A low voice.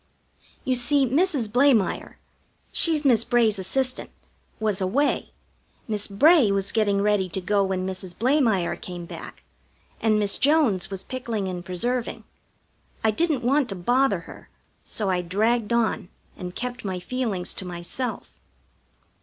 No: high, 215 Hz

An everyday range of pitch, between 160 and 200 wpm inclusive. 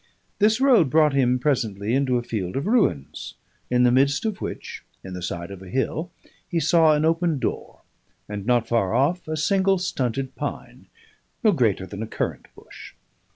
No: wide, 6.7 semitones; average, 180 wpm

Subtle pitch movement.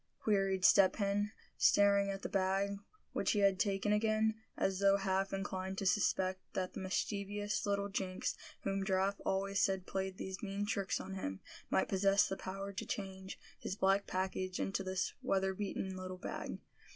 Yes: narrow, 0.9 semitones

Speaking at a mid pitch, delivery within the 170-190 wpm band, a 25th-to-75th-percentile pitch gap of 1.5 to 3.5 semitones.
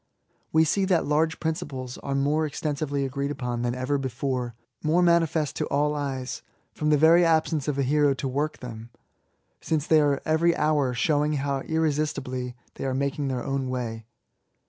Yes: medium, 145 Hz; average, 175 wpm; average, 2.9 semitones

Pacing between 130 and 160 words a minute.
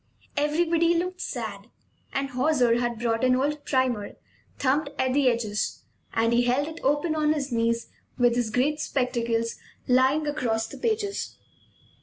Yes: average, 150 wpm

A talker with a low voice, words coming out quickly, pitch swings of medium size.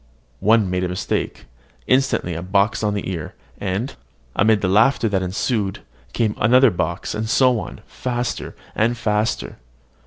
No: low, 105 Hz; average, 150 wpm; average, 4.0 semitones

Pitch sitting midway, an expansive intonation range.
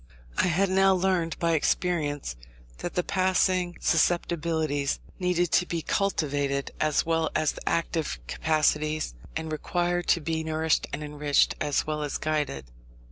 No: medium, 160 Hz; average, 2.8 semitones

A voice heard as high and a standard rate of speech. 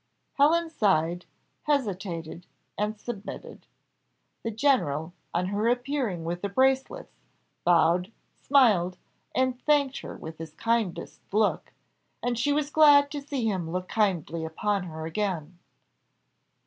No: high, 210 Hz; slow, 120 wpm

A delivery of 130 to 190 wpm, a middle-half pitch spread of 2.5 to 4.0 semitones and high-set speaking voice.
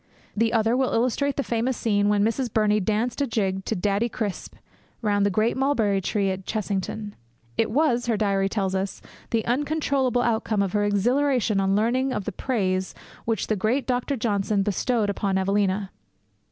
Yes: average, 175 wpm; average, 3.4 semitones; high, 215 Hz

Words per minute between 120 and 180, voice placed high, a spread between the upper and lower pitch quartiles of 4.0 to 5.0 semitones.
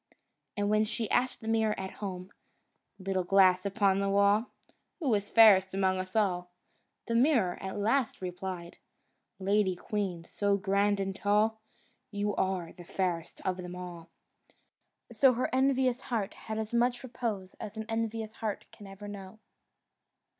No: average, 155 wpm; high, 200 Hz; average, 2.8 semitones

